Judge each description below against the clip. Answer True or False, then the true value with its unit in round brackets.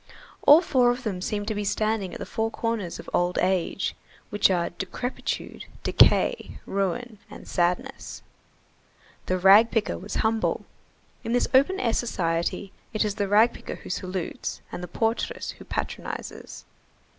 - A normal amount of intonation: True (3.8 semitones)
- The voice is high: True (210 Hz)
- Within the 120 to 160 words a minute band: True (155 wpm)